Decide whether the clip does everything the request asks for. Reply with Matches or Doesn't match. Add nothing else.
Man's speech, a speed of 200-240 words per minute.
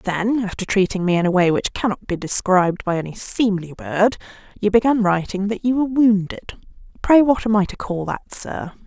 Doesn't match